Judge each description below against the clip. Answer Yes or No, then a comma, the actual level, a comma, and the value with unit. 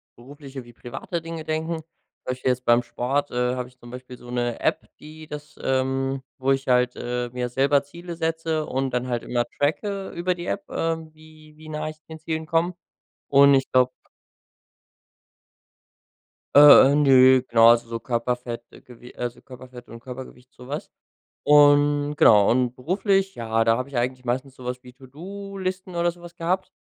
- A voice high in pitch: No, low, 135 Hz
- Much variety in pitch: No, average, 4.2 semitones